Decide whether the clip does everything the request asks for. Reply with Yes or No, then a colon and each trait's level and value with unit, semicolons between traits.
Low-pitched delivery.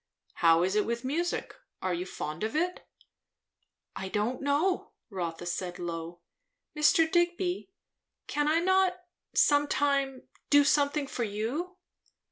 No: very high, 275 Hz